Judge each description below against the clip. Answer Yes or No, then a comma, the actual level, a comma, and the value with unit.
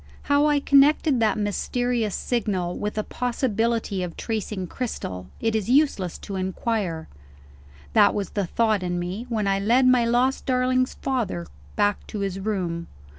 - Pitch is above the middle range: Yes, high, 215 Hz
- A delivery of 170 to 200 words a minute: No, average, 155 wpm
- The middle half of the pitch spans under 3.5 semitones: No, average, 4.5 semitones